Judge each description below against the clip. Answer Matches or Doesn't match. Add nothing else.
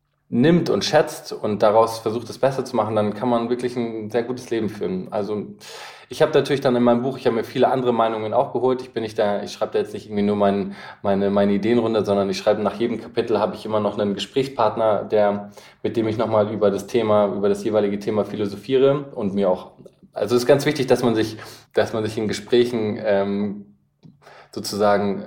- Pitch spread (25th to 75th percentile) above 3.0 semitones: Doesn't match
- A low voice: Matches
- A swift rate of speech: Matches